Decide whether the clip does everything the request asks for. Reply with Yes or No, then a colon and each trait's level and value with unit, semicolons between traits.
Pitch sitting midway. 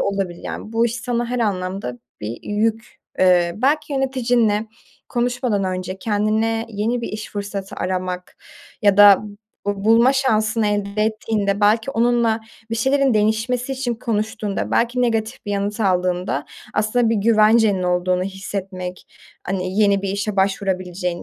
No: high, 210 Hz